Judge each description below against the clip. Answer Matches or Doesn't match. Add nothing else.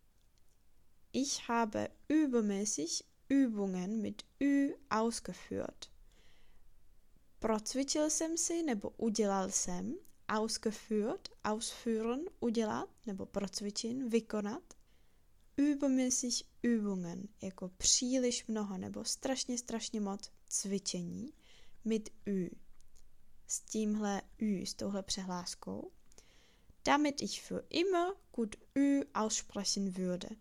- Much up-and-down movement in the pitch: Doesn't match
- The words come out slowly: Matches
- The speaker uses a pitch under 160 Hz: Doesn't match